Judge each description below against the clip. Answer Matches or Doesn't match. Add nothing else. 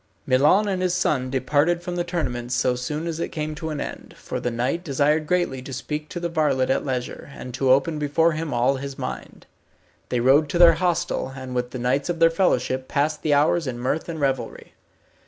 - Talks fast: Matches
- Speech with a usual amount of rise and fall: Matches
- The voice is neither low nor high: Matches